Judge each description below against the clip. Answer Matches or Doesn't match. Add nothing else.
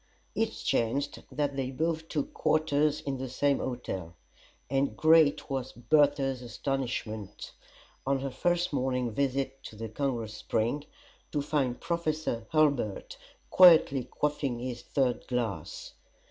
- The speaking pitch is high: Doesn't match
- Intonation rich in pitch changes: Doesn't match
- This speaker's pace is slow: Matches